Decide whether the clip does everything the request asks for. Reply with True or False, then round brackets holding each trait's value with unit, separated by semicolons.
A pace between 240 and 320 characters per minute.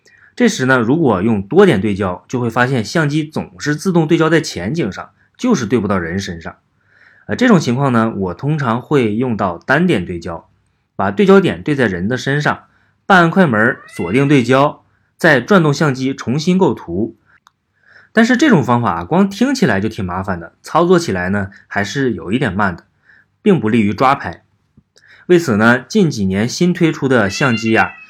True (265 characters per minute)